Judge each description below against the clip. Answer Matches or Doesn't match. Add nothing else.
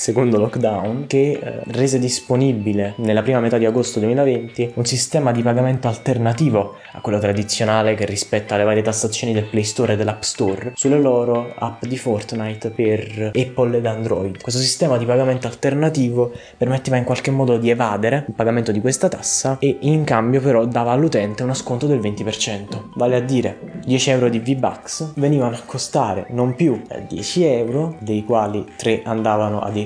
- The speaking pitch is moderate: Doesn't match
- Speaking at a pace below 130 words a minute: Doesn't match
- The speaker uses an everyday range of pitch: Matches